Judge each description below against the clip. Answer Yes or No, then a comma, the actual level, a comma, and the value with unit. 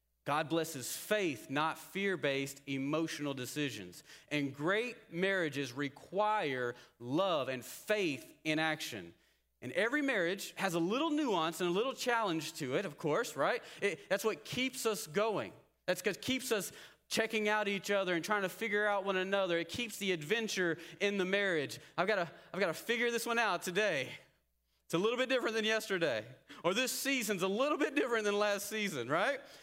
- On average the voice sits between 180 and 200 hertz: Yes, high, 190 Hz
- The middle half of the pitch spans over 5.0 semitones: Yes, wide, 5.6 semitones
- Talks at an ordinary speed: Yes, average, 180 wpm